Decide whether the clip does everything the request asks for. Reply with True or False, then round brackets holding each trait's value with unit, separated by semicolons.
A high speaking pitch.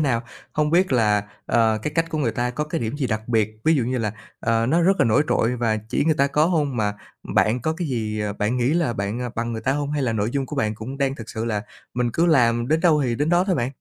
False (125 Hz)